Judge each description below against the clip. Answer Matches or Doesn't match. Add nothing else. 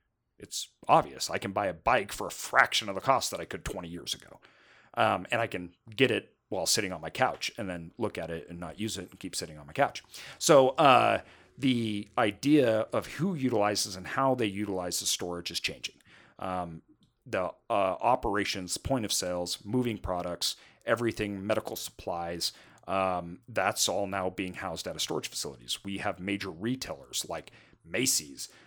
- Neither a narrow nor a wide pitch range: Matches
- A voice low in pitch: Matches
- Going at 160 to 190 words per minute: Matches